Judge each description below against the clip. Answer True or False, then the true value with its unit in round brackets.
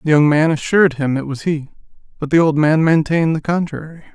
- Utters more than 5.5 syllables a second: True (6.0 syllables/s)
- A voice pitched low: False (155 Hz)